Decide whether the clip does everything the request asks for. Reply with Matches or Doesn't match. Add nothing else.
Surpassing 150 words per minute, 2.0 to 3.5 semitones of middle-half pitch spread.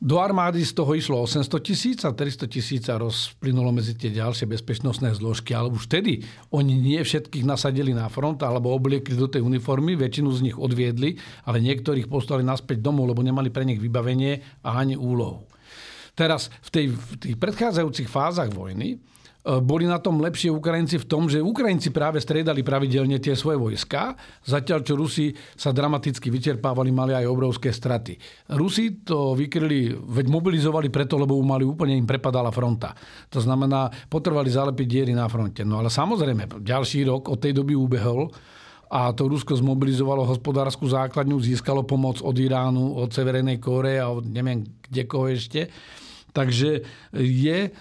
Matches